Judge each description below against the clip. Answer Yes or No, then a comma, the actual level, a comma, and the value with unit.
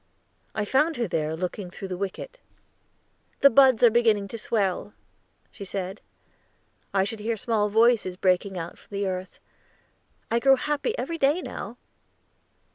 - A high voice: Yes, high, 210 Hz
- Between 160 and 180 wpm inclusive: No, average, 150 wpm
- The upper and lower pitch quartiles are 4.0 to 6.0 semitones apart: Yes, average, 4.3 semitones